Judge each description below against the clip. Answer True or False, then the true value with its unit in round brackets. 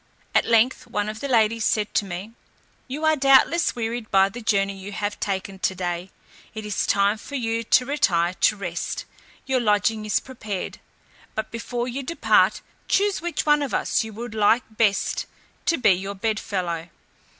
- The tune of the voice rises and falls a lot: False (3.9 semitones)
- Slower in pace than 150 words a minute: False (170 wpm)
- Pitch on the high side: True (215 Hz)